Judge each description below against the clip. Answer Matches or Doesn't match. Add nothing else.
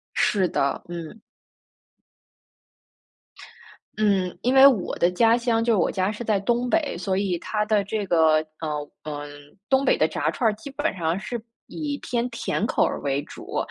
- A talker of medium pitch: Doesn't match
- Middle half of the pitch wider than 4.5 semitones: Matches